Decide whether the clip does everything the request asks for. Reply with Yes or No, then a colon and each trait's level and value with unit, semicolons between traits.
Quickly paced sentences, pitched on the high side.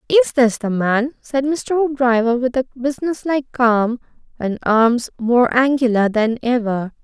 No: average, 155 wpm; very high, 250 Hz